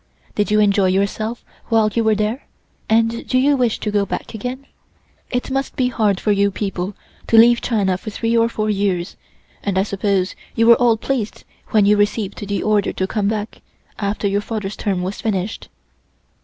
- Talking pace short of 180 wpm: No, average, 190 wpm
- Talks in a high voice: Yes, high, 210 Hz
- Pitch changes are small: Yes, narrow, 2.3 semitones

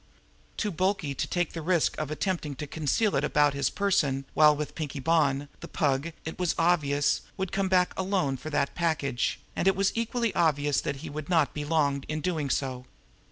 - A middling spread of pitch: Yes, average, 4.1 semitones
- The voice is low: No, medium, 155 Hz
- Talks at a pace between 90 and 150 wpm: No, average, 200 wpm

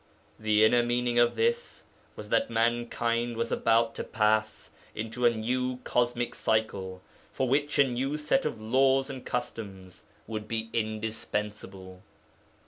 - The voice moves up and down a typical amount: No, narrow, 2.2 semitones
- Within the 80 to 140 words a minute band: Yes, slow, 135 wpm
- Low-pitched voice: Yes, low, 115 Hz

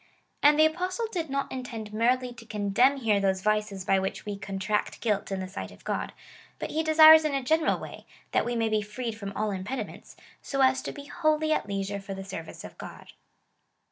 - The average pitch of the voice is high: Yes, high, 225 Hz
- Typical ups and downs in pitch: No, wide, 6.1 semitones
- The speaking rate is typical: No, fast, 215 wpm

